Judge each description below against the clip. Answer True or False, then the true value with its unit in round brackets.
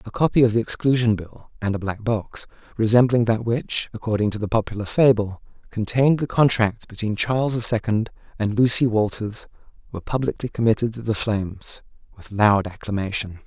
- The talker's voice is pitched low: True (110 Hz)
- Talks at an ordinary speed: True (165 wpm)